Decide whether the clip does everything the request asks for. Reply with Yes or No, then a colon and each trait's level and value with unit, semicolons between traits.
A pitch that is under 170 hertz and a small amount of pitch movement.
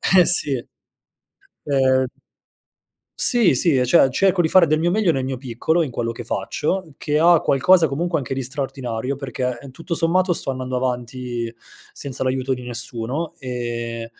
No: low, 135 Hz; average, 4.9 semitones